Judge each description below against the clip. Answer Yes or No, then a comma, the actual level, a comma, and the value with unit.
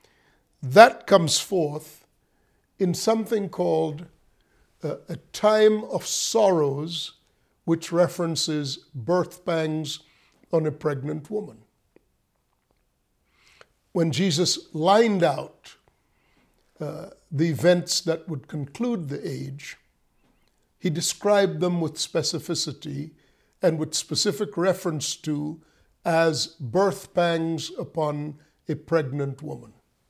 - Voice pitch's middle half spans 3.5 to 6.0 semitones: No, average, 2.7 semitones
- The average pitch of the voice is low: No, medium, 165 Hz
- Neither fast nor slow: No, slow, 95 wpm